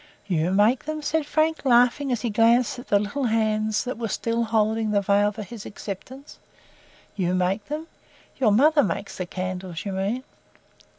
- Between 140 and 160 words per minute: No, average, 175 wpm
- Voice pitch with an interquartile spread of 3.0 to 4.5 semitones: Yes, average, 4.0 semitones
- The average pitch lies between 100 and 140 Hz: No, high, 220 Hz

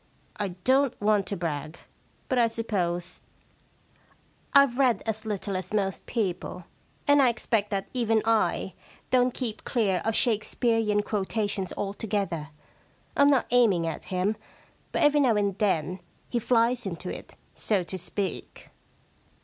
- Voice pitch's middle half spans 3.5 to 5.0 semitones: Yes, average, 3.8 semitones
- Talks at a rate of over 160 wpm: No, average, 140 wpm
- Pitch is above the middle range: Yes, high, 210 Hz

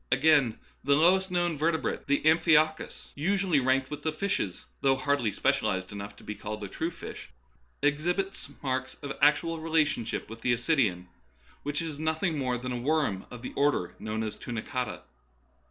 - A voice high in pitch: No, medium, 140 Hz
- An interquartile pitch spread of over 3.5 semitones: Yes, average, 4.7 semitones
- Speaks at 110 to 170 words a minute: Yes, average, 160 wpm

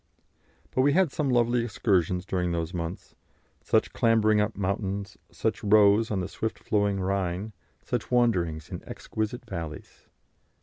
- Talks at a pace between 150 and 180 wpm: No, average, 140 wpm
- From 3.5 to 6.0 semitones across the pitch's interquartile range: Yes, average, 3.8 semitones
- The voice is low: Yes, low, 100 Hz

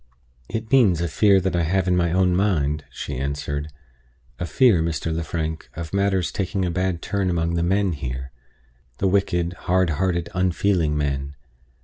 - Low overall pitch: Yes, very low, 85 Hz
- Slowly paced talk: No, average, 165 wpm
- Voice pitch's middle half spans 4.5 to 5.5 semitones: No, average, 3.2 semitones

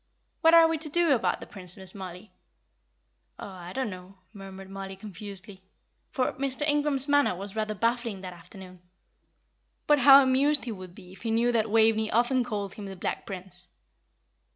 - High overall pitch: Yes, high, 215 Hz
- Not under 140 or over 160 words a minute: No, average, 175 wpm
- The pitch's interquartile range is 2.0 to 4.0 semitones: No, wide, 5.6 semitones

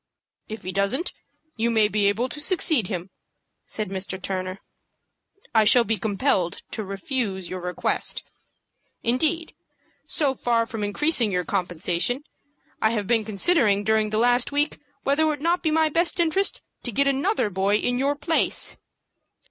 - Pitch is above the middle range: Yes, high, 225 Hz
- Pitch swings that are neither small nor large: No, wide, 6.2 semitones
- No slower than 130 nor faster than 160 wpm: Yes, average, 155 wpm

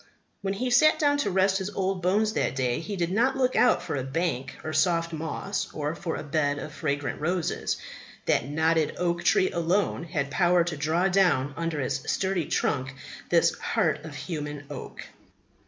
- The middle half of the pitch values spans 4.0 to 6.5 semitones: Yes, average, 4.5 semitones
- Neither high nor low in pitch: Yes, medium, 170 Hz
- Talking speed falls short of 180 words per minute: No, average, 185 wpm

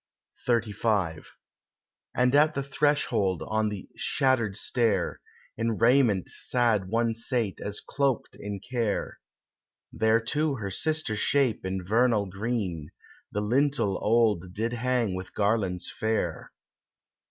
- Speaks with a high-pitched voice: No, low, 110 Hz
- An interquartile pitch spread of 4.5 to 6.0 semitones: No, average, 3.8 semitones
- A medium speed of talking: No, slow, 120 wpm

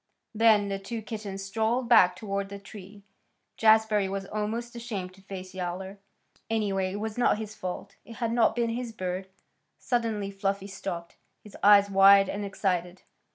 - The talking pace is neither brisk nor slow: Yes, average, 160 wpm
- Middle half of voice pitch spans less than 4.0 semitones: Yes, narrow, 2.4 semitones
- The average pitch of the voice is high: Yes, high, 200 Hz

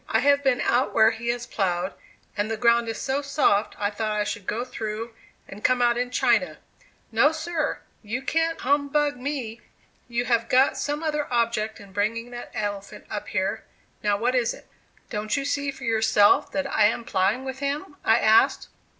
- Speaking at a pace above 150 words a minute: Yes, average, 190 wpm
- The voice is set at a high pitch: Yes, high, 235 Hz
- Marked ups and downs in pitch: No, average, 4.2 semitones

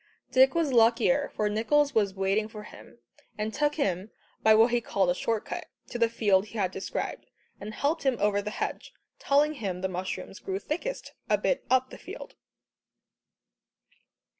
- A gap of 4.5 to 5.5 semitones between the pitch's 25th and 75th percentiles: Yes, average, 5.1 semitones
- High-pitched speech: Yes, high, 220 Hz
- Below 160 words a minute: No, average, 175 wpm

